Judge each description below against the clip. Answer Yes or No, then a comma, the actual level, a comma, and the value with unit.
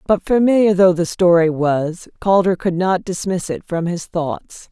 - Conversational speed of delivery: Yes, average, 180 wpm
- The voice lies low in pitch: No, medium, 180 Hz